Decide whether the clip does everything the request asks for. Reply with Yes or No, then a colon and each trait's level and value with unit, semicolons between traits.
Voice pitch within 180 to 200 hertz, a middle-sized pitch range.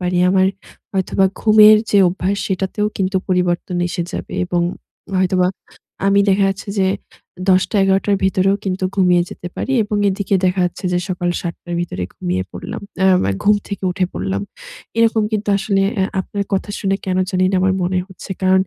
No: high, 190 Hz; narrow, 1.7 semitones